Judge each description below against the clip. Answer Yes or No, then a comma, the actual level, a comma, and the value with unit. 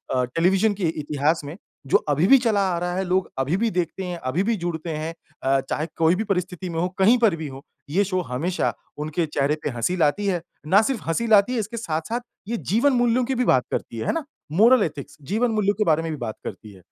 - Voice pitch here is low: No, medium, 180 Hz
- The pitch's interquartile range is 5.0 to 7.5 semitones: Yes, wide, 5.6 semitones